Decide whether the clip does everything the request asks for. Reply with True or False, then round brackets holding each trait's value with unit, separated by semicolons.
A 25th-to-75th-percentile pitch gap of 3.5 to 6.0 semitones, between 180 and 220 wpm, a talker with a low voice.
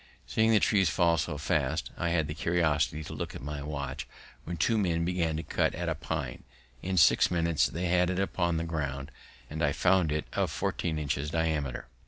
False (2.8 semitones; 205 wpm; 80 Hz)